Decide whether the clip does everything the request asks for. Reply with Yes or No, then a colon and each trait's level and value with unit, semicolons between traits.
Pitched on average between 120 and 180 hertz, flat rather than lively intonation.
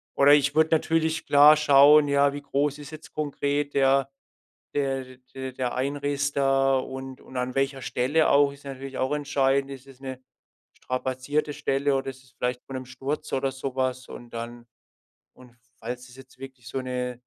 Yes: low, 135 Hz; narrow, 1.7 semitones